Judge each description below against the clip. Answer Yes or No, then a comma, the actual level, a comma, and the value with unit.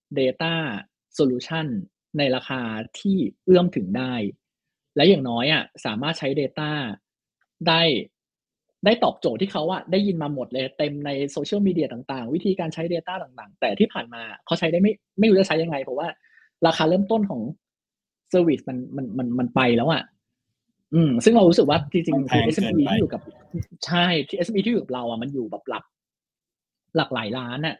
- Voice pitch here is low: No, medium, 160 Hz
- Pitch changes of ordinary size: No, wide, 5.8 semitones